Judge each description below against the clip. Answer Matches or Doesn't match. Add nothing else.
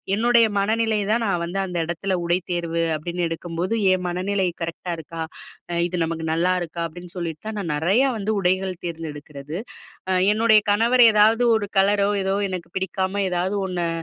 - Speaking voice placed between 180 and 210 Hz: Matches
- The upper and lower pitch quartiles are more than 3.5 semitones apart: Doesn't match